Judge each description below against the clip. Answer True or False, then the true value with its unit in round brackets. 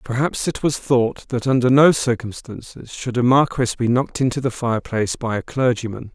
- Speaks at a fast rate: False (185 wpm)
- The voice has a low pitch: True (120 Hz)